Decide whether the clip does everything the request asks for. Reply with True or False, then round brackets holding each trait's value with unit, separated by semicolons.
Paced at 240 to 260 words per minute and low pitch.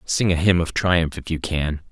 True (250 wpm; 85 Hz)